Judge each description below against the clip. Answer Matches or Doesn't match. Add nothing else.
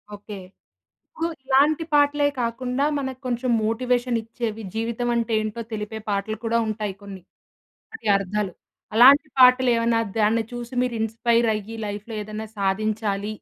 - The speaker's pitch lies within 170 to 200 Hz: Doesn't match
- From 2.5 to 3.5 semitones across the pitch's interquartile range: Matches